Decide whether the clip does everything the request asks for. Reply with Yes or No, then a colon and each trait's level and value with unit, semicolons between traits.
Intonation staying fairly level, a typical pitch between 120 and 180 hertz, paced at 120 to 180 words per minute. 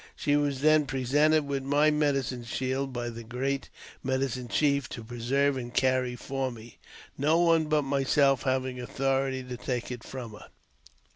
Yes: narrow, 2.2 semitones; low, 135 Hz; average, 165 wpm